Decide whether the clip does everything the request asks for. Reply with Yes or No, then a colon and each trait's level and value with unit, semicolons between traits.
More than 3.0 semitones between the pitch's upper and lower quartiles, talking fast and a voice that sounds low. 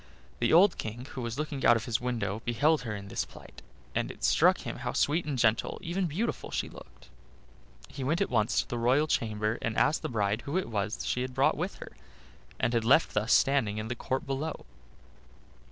Yes: average, 4.8 semitones; fast, 215 wpm; low, 120 Hz